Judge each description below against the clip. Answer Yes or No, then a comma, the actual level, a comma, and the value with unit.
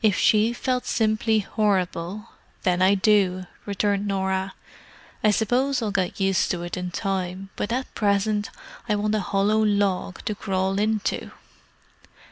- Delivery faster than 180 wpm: No, average, 145 wpm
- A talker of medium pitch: No, high, 200 Hz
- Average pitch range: No, narrow, 2.2 semitones